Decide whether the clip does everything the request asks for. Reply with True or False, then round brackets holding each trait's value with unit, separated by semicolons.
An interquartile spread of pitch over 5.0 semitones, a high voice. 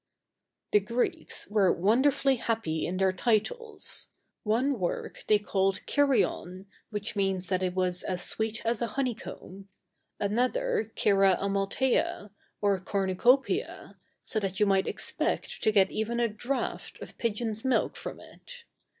False (4.0 semitones; 210 Hz)